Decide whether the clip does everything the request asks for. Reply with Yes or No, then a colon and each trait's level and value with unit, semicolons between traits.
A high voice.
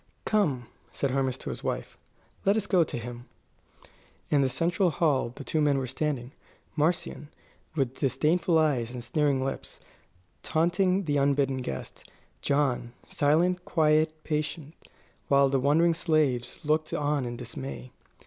No: medium, 145 Hz